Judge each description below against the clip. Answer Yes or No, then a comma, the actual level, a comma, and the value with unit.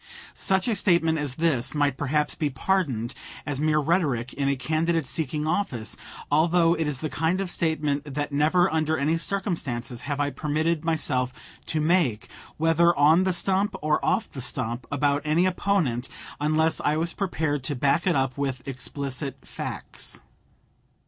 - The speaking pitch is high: No, medium, 150 Hz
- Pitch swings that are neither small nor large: Yes, average, 3.2 semitones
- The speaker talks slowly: No, average, 160 wpm